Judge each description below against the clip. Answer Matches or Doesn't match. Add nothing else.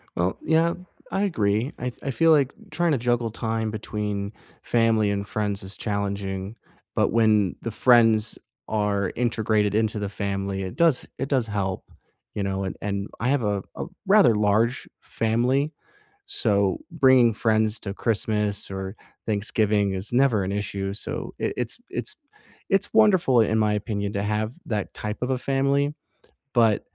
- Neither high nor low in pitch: Doesn't match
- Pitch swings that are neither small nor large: Matches